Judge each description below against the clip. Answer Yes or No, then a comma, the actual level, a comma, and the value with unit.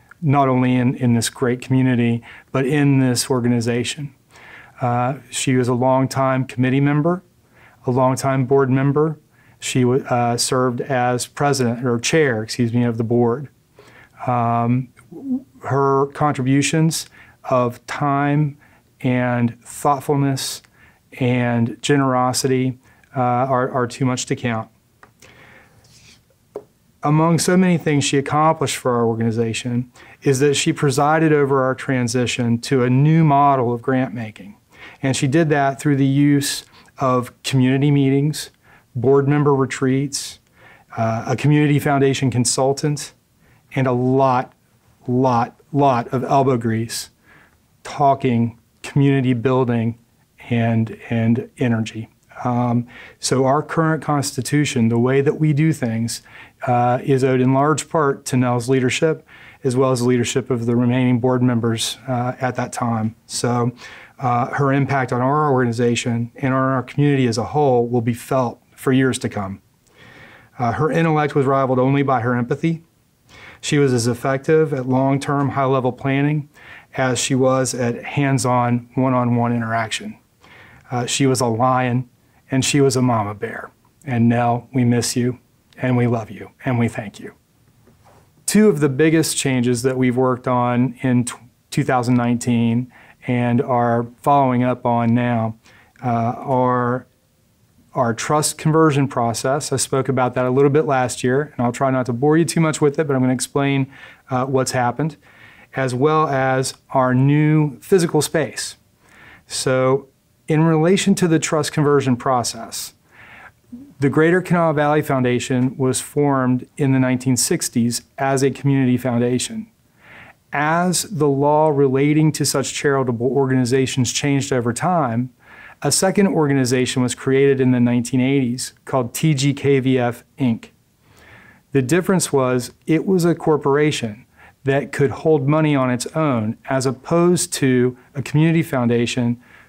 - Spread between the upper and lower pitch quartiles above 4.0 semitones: No, narrow, 2.6 semitones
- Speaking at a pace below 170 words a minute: Yes, average, 145 wpm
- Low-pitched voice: Yes, low, 130 Hz